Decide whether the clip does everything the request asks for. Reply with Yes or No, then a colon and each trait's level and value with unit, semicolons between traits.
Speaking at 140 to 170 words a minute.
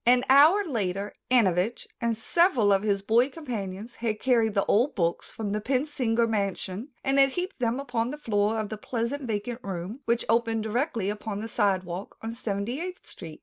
No: average, 185 wpm